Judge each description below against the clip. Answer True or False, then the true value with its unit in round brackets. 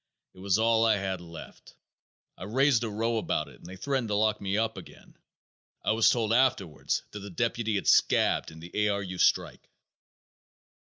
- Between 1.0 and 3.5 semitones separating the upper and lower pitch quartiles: True (3.1 semitones)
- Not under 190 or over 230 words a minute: True (195 wpm)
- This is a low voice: True (105 Hz)